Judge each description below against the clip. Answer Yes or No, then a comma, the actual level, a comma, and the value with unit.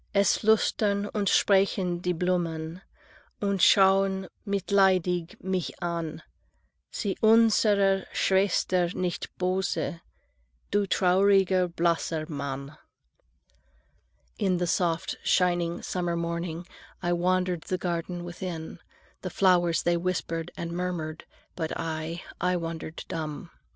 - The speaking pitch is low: No, medium, 180 Hz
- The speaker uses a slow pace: Yes, slow, 105 wpm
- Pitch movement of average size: No, narrow, 2.3 semitones